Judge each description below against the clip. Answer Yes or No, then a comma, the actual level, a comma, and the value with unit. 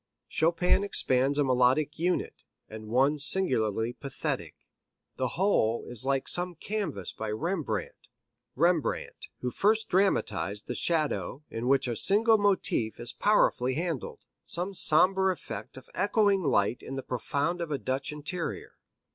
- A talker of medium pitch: Yes, medium, 150 Hz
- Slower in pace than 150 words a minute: Yes, average, 140 wpm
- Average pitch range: No, wide, 6.4 semitones